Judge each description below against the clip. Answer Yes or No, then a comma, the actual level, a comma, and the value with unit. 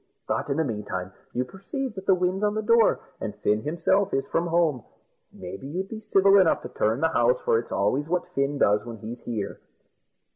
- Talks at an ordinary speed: No, fast, 215 wpm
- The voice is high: No, medium, 150 Hz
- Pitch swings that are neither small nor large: No, wide, 8.6 semitones